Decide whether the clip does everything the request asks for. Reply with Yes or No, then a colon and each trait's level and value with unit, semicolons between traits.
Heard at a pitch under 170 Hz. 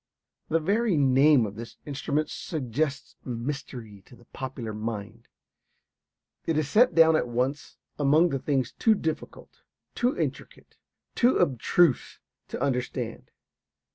Yes: medium, 140 Hz